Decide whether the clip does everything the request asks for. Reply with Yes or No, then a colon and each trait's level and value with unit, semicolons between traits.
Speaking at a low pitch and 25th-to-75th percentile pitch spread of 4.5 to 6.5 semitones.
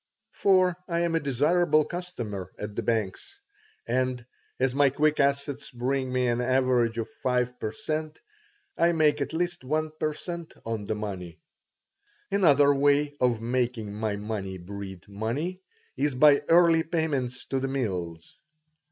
Yes: low, 130 Hz; wide, 5.4 semitones